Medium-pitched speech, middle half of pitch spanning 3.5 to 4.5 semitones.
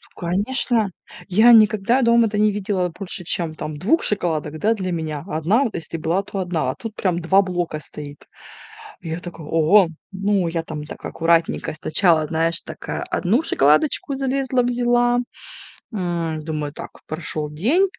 No: medium, 180 Hz; average, 5.2 semitones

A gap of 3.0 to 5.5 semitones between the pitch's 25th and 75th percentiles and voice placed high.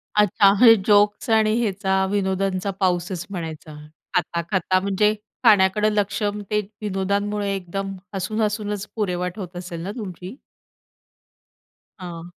No: narrow, 2.4 semitones; high, 195 Hz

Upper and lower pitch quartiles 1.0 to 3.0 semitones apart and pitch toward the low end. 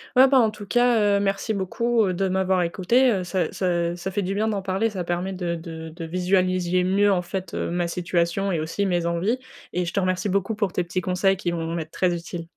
No: narrow, 2.4 semitones; medium, 185 Hz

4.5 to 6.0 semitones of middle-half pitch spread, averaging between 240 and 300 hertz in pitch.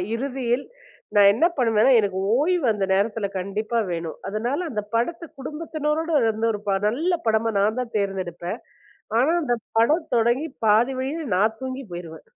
No: average, 4.9 semitones; high, 230 Hz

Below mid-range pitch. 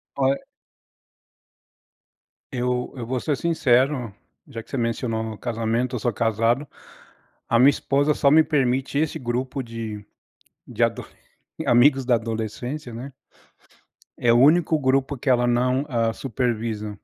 Yes: low, 125 Hz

